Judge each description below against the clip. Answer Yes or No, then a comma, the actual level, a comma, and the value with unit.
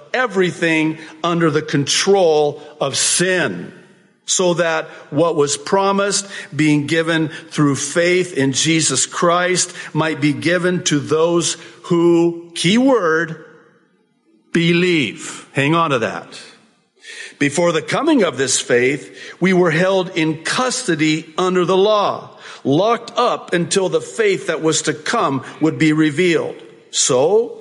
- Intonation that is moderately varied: Yes, average, 3.2 semitones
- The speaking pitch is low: No, medium, 170 Hz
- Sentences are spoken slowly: Yes, slow, 125 wpm